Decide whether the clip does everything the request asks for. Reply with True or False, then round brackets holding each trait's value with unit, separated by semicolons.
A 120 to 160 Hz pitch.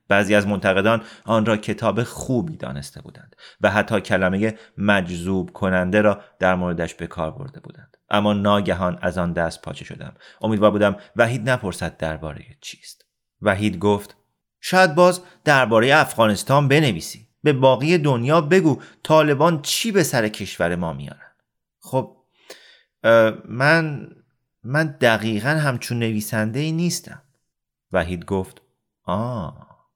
False (110 Hz)